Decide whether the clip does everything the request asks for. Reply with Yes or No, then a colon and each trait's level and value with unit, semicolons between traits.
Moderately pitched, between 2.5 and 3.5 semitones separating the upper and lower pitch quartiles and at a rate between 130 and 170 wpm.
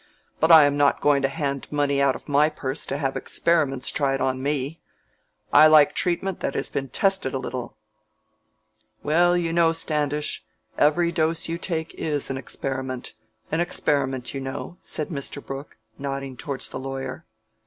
Yes: medium, 145 Hz; average, 2.9 semitones; average, 165 wpm